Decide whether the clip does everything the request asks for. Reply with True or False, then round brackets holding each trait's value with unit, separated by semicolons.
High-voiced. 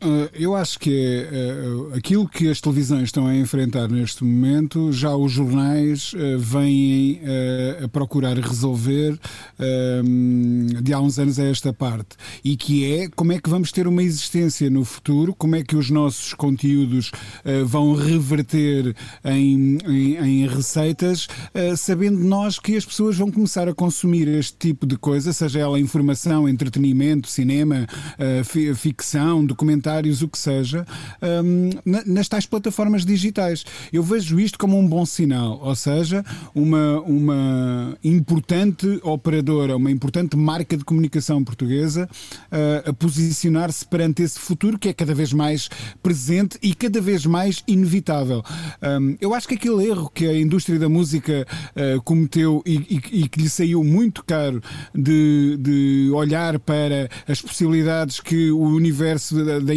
False (150 Hz)